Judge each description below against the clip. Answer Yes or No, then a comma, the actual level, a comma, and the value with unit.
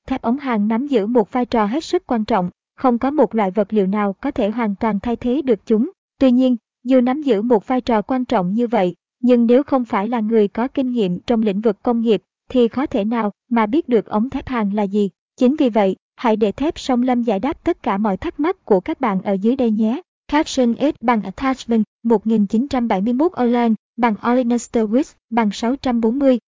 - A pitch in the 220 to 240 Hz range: Yes, high, 235 Hz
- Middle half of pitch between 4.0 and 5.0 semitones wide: No, average, 2.9 semitones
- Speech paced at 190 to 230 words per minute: Yes, average, 220 wpm